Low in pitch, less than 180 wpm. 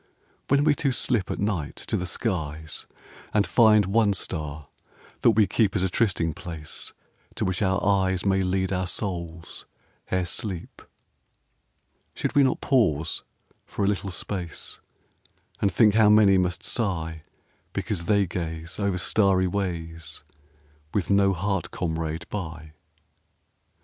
Yes: very low, 95 Hz; average, 140 wpm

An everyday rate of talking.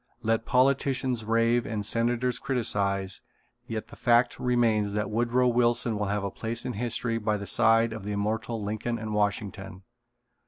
Yes: average, 160 wpm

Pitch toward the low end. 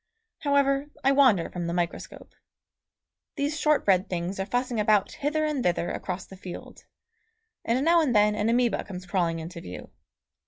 No: high, 210 Hz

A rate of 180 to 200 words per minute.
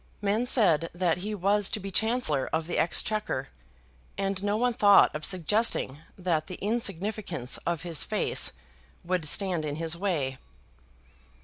No: average, 145 wpm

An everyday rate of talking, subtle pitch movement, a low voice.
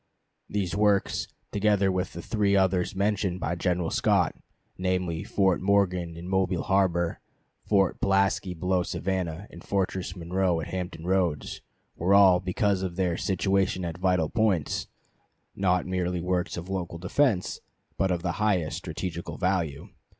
Yes: average, 145 wpm; narrow, 1.8 semitones; very low, 90 Hz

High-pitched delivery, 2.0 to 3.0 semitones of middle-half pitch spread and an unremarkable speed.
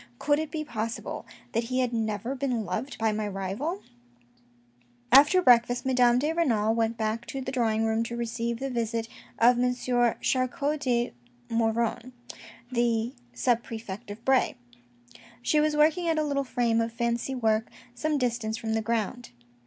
Yes: high, 235 Hz; average, 2.7 semitones; average, 170 wpm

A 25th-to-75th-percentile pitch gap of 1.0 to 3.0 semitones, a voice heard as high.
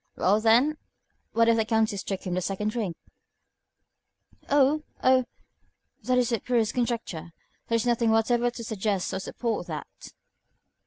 Yes: narrow, 2.6 semitones; high, 230 Hz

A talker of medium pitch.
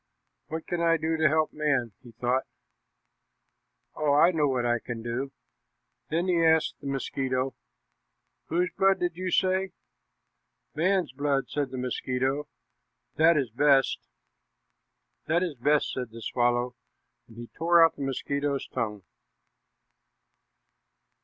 Yes: medium, 145 Hz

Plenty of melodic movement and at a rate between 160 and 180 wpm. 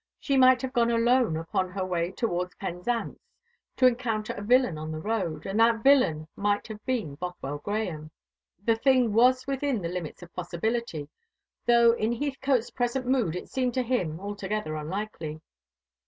Yes: wide, 5.9 semitones; average, 165 wpm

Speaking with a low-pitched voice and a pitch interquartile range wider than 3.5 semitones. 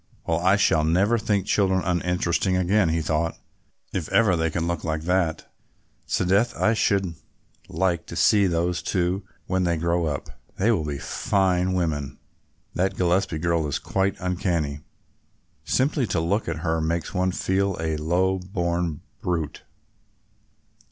No: very low, 90 Hz; narrow, 2.6 semitones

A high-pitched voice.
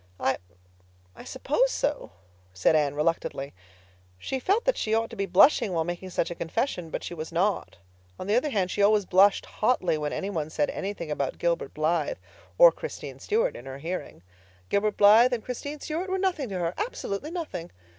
Yes: high, 195 Hz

